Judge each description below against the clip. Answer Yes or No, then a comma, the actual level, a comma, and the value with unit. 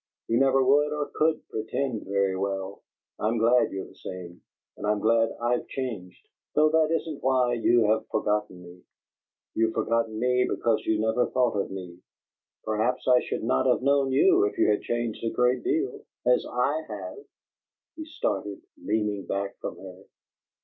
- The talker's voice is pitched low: Yes, low, 115 Hz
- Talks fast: No, average, 170 wpm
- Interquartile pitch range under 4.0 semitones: No, average, 4.7 semitones